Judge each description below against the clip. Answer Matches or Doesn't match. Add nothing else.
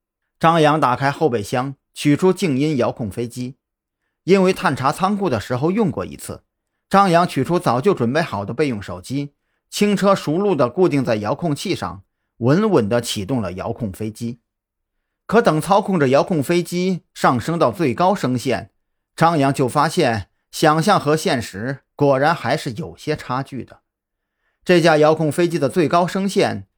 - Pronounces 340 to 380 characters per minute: Doesn't match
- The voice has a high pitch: Doesn't match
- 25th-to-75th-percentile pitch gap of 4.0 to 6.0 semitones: Doesn't match